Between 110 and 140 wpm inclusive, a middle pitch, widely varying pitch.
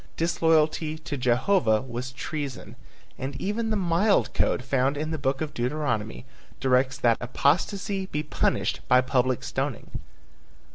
No: slow, 135 wpm; medium, 145 Hz; average, 4.2 semitones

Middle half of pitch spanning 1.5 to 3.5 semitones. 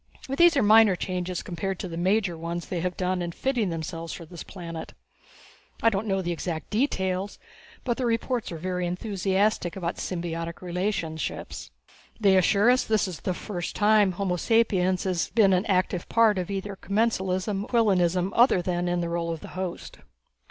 Yes: average, 3.0 semitones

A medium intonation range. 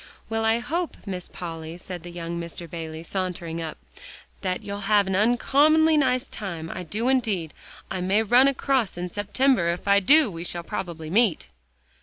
No: wide, 5.9 semitones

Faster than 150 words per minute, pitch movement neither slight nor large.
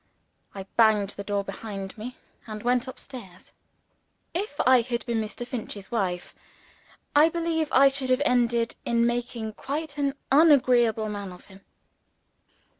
No: average, 145 wpm; average, 4.3 semitones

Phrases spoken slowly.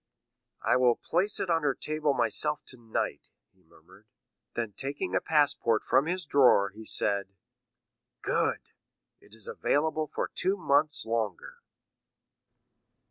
Yes: slow, 125 wpm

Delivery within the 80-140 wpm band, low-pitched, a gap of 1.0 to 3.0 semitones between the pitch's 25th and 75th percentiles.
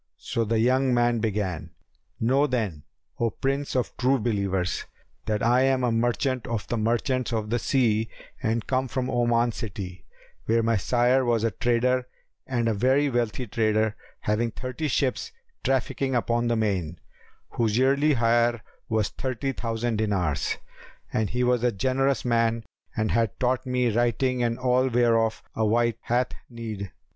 No: average, 155 wpm; low, 120 Hz; narrow, 2.5 semitones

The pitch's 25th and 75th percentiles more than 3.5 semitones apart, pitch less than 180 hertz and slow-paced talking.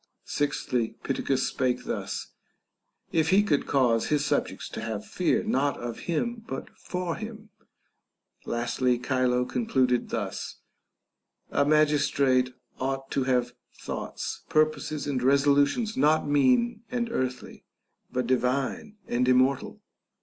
Yes: average, 4.0 semitones; medium, 140 Hz; slow, 120 wpm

